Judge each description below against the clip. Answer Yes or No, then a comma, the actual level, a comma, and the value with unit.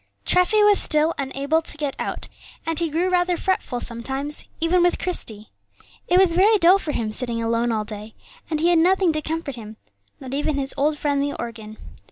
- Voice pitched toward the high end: Yes, very high, 300 Hz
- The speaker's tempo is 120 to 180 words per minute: No, average, 200 wpm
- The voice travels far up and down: Yes, wide, 6.5 semitones